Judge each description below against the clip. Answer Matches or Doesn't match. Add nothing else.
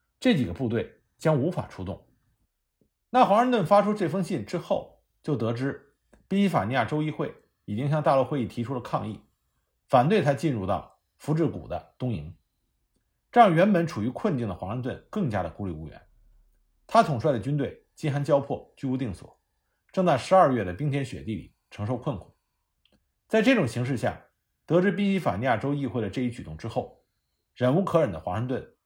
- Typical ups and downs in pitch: Doesn't match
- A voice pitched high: Doesn't match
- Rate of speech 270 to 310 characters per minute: Matches